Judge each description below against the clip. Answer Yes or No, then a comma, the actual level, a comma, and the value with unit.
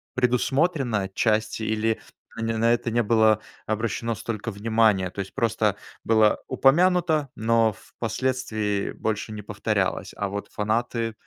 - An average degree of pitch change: No, narrow, 1.9 semitones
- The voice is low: Yes, low, 110 Hz